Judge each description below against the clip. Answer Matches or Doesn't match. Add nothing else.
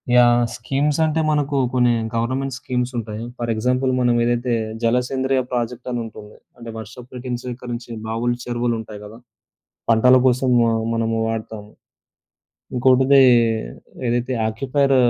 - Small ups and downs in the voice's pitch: Matches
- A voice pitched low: Matches